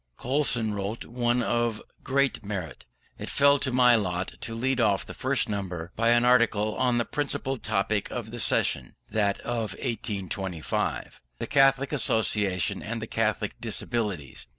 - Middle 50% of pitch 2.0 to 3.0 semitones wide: No, average, 3.4 semitones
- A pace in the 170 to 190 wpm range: No, average, 150 wpm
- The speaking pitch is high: No, low, 115 Hz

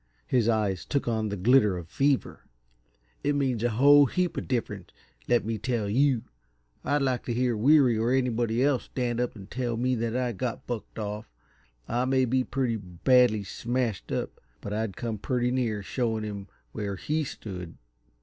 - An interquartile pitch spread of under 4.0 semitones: Yes, average, 3.2 semitones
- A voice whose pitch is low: Yes, low, 120 Hz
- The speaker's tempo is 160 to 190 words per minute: Yes, average, 180 wpm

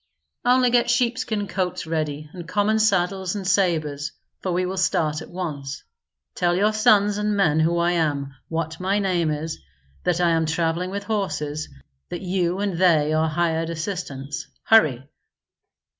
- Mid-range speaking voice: Yes, medium, 175 Hz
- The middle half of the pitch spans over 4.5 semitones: No, average, 3.9 semitones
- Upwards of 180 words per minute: No, average, 160 wpm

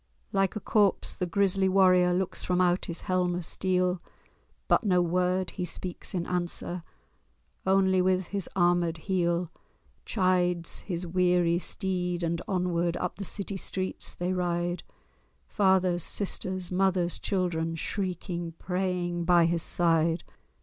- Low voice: No, medium, 180 Hz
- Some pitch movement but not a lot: No, narrow, 1.3 semitones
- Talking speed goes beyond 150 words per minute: No, slow, 135 wpm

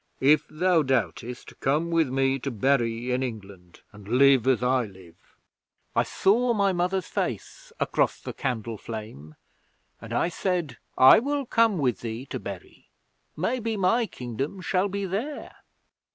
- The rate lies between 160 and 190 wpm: No, average, 150 wpm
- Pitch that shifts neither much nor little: No, wide, 8.2 semitones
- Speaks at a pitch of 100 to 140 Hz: Yes, low, 135 Hz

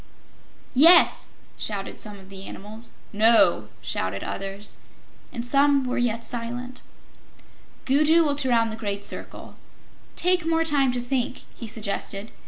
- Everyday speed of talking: No, slow, 130 wpm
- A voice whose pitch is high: Yes, high, 235 Hz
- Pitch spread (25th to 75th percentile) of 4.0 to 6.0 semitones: Yes, average, 5.2 semitones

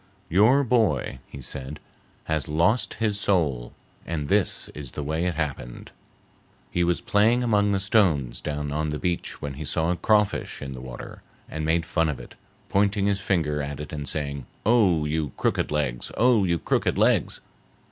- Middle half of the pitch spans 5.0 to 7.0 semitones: Yes, wide, 5.5 semitones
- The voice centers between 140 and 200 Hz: No, very low, 80 Hz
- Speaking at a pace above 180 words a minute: No, average, 175 wpm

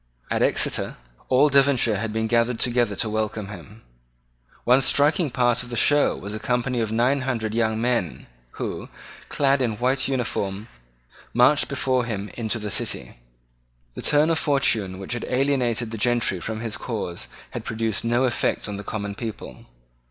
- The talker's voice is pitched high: No, low, 115 Hz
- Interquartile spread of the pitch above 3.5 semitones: No, average, 3.0 semitones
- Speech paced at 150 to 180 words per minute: Yes, average, 170 wpm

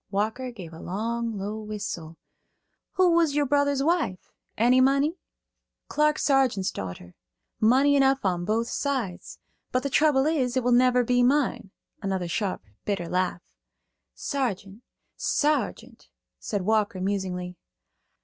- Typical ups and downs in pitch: No, wide, 6.0 semitones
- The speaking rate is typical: No, slow, 130 wpm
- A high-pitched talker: Yes, high, 235 Hz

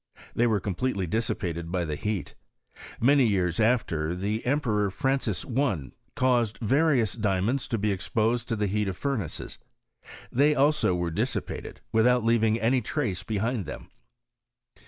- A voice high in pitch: No, low, 110 Hz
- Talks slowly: No, average, 150 wpm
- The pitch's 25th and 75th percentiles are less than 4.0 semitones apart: No, average, 4.6 semitones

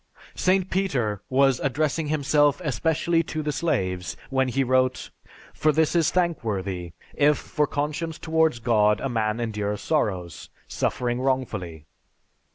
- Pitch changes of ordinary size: No, wide, 6.3 semitones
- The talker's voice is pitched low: Yes, low, 130 Hz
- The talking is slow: Yes, slow, 130 wpm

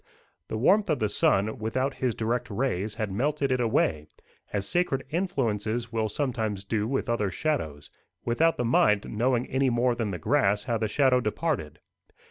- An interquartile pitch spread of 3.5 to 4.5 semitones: Yes, average, 4.1 semitones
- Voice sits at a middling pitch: No, low, 115 Hz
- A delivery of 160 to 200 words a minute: Yes, average, 170 wpm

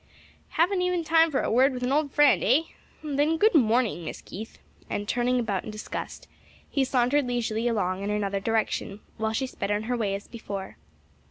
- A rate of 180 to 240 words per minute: Yes, average, 190 wpm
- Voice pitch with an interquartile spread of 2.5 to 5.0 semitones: No, wide, 5.4 semitones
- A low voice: No, high, 240 Hz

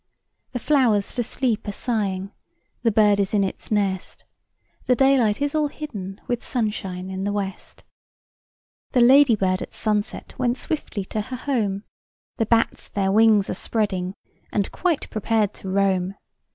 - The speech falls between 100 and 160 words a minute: Yes, average, 150 wpm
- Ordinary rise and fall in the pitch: Yes, average, 3.9 semitones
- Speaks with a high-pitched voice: Yes, high, 210 Hz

